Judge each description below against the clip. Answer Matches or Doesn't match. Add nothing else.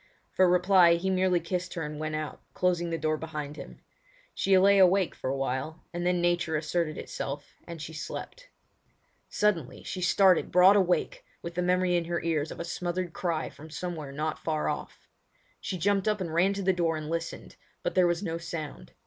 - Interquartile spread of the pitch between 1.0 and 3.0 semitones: Matches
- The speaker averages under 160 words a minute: Doesn't match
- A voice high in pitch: Doesn't match